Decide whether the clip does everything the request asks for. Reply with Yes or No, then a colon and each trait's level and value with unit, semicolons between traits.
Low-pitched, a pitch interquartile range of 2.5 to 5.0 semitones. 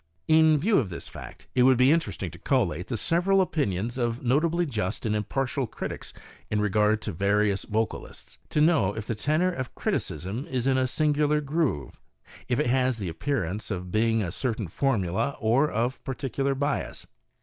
No: low, 125 Hz; wide, 5.4 semitones